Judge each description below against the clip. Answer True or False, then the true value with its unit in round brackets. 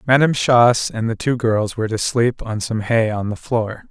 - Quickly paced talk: True (230 wpm)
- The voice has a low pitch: True (115 Hz)